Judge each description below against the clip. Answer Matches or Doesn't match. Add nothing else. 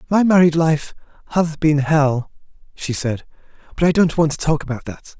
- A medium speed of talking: Matches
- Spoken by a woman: Doesn't match